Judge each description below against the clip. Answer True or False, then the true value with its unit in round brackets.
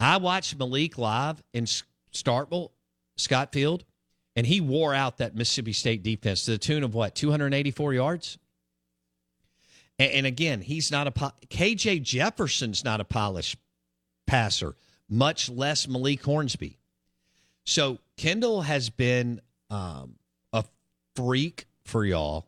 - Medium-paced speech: False (125 wpm)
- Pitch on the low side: True (125 Hz)